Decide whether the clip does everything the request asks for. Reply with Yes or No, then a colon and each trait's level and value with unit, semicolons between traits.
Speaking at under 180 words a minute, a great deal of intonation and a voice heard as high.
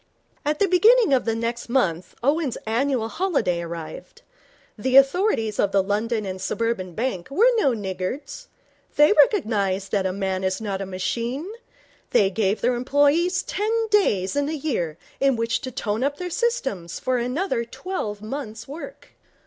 Yes: average, 160 wpm; wide, 6.6 semitones; high, 235 Hz